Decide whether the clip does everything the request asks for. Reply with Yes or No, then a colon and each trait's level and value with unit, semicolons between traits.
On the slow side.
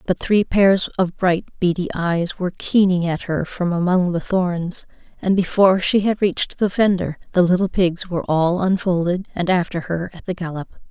No: average, 185 wpm